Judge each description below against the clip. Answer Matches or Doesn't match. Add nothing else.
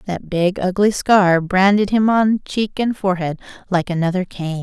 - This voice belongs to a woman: Matches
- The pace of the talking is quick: Doesn't match